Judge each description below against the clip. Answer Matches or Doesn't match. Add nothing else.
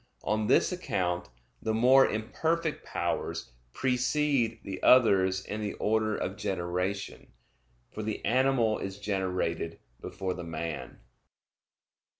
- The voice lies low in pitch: Matches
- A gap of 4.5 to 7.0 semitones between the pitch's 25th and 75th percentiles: Matches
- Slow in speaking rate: Matches